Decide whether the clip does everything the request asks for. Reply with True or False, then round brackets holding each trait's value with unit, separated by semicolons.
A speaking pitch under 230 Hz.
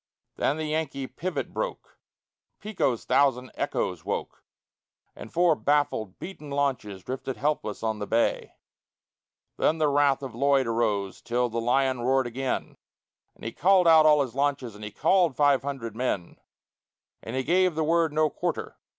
True (135 Hz)